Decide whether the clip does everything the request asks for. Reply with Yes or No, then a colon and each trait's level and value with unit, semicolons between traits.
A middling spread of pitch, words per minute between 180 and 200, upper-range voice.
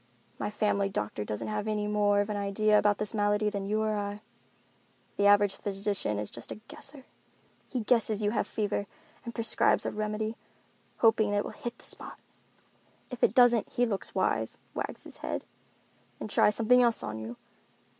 No: narrow, 1.3 semitones; average, 185 wpm; high, 210 Hz